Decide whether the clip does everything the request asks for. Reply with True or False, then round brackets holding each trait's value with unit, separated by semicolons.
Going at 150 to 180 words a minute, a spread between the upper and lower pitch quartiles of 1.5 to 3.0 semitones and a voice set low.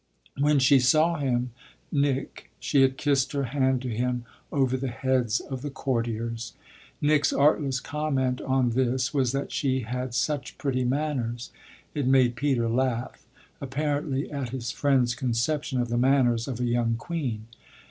True (155 wpm; 2.5 semitones; 130 Hz)